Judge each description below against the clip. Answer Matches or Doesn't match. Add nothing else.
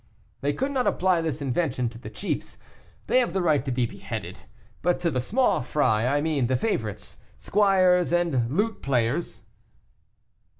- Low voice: Doesn't match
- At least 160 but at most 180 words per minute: Matches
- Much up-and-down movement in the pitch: Matches